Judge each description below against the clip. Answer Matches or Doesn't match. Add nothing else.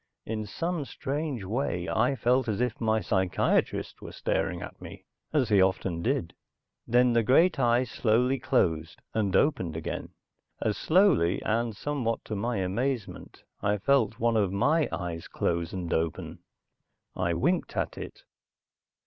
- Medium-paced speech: Matches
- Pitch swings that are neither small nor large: Doesn't match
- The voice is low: Matches